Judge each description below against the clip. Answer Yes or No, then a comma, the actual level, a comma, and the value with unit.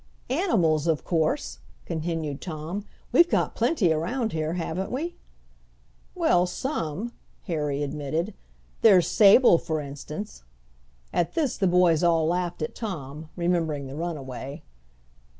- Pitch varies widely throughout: No, average, 3.9 semitones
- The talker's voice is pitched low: No, medium, 165 Hz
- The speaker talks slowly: Yes, slow, 120 wpm